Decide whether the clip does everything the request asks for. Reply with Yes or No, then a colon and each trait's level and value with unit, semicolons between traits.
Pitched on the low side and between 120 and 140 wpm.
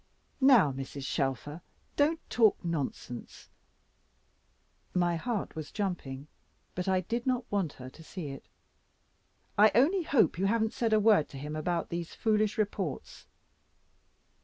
No: medium, 185 Hz; slow, 135 wpm